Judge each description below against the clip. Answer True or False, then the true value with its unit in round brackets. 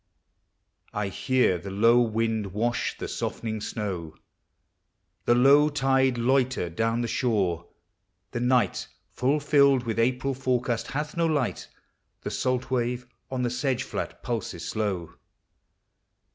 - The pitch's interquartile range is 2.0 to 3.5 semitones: True (3.2 semitones)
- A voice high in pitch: False (120 Hz)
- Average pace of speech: False (130 wpm)